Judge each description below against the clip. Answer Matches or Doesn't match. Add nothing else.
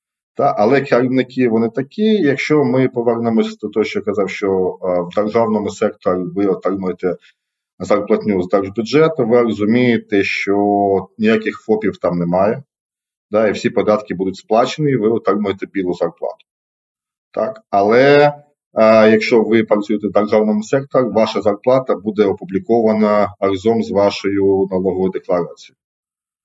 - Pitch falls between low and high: Doesn't match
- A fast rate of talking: Doesn't match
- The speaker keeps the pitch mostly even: Doesn't match